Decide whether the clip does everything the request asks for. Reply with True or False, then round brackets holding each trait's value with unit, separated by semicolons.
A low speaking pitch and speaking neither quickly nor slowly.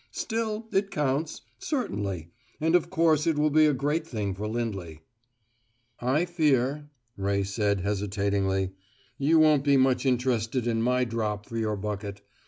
True (125 Hz; 150 wpm)